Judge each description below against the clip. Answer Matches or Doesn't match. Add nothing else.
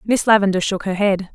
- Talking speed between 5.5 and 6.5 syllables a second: Matches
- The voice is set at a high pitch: Matches